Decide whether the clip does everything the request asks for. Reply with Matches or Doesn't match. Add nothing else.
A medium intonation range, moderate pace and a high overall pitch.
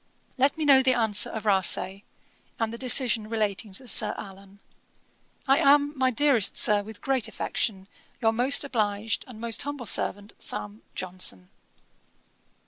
Matches